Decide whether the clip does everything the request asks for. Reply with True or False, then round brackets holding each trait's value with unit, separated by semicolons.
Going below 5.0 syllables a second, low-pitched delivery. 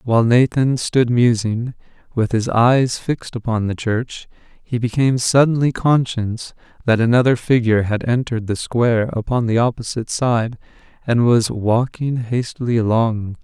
True (4.7 syllables/s; 120 Hz)